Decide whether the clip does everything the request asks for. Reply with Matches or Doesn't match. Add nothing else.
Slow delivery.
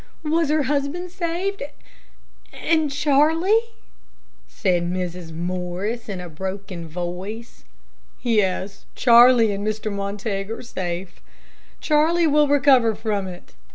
Matches